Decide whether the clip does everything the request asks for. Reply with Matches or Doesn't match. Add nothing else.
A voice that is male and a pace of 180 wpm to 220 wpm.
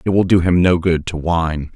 Doesn't match